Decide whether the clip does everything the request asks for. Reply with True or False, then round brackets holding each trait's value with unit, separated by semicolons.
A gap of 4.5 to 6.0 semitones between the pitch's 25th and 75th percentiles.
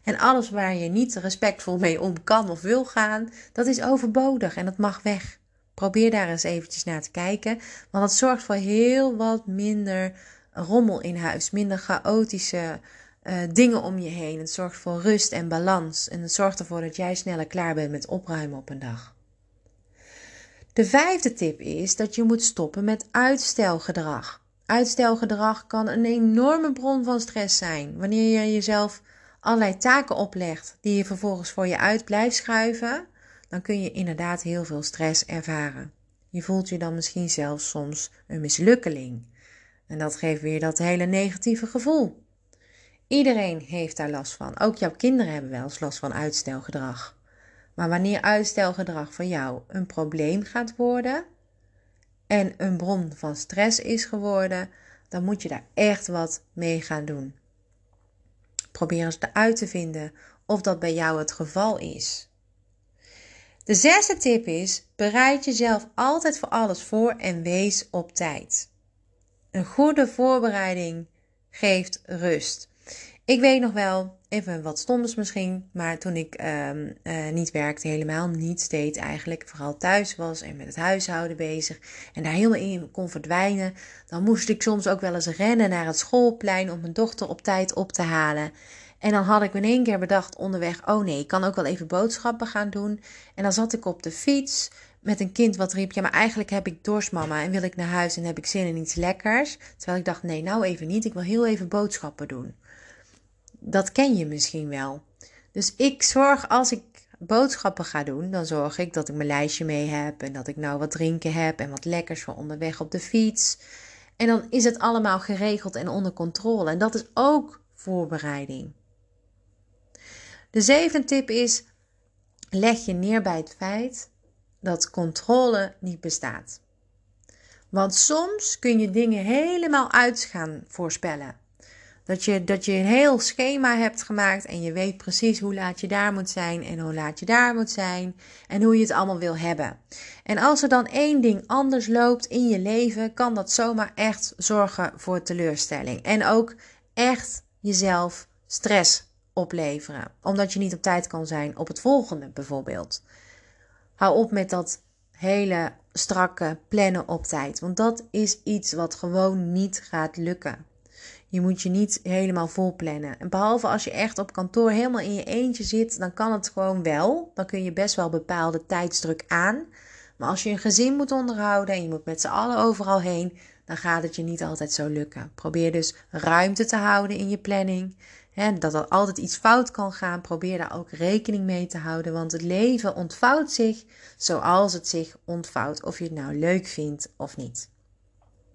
True (5.2 semitones)